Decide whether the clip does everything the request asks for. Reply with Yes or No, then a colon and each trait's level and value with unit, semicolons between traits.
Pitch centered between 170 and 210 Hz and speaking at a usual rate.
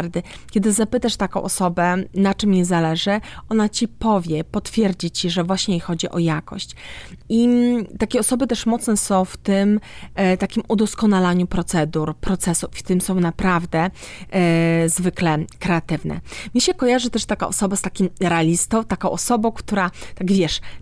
Yes: high, 190 Hz; average, 150 wpm